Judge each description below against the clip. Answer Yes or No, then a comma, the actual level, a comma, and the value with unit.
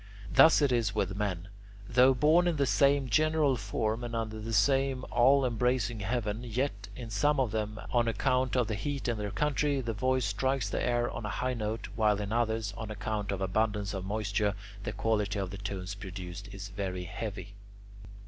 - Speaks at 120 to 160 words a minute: No, average, 190 wpm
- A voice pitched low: Yes, low, 110 Hz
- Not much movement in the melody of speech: No, average, 3.7 semitones